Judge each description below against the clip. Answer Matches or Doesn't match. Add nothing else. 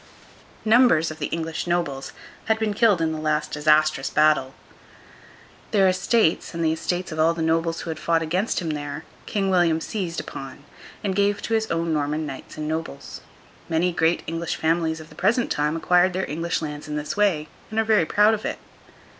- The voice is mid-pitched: Matches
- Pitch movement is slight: Doesn't match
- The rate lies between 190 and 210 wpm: Matches